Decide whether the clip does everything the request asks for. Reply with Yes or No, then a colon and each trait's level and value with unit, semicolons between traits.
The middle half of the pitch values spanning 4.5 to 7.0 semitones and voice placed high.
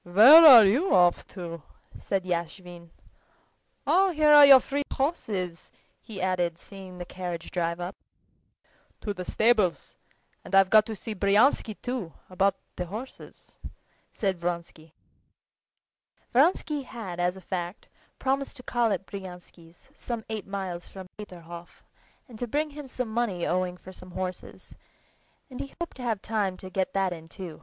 Yes: average, 5.2 semitones; high, 195 Hz